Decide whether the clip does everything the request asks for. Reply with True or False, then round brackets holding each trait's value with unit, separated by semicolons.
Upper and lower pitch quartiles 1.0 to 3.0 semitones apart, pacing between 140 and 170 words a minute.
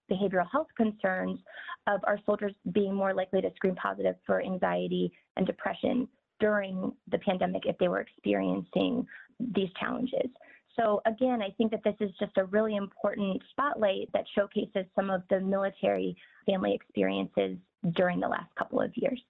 False (3.8 semitones; 160 wpm)